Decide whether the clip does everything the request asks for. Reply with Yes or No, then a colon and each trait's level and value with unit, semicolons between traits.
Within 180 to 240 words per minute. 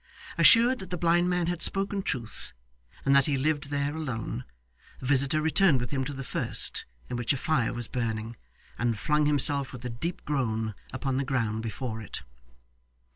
Yes: average, 185 wpm